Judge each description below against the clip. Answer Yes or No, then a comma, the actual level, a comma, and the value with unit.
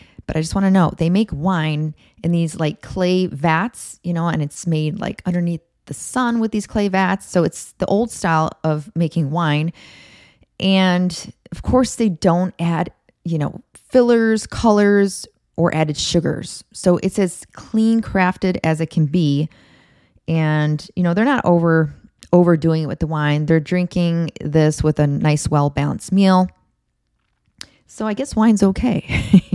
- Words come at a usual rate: Yes, average, 165 wpm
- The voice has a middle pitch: Yes, medium, 175 Hz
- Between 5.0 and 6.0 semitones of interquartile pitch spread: No, average, 3.7 semitones